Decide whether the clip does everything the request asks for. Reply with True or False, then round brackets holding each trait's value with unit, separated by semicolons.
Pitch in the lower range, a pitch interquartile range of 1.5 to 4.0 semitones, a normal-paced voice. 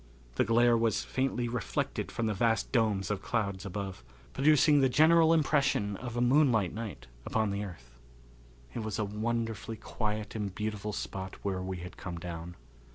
True (110 Hz; 3.6 semitones; 165 wpm)